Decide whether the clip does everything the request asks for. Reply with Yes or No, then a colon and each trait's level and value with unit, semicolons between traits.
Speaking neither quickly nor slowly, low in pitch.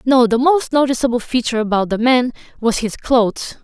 No: average, 180 wpm; high, 245 Hz